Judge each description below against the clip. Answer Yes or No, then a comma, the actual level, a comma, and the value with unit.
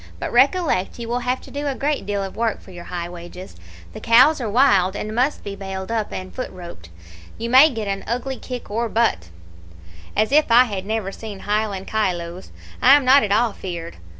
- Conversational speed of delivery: No, fast, 210 wpm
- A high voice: Yes, high, 215 Hz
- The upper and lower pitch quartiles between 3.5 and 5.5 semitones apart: Yes, average, 4.7 semitones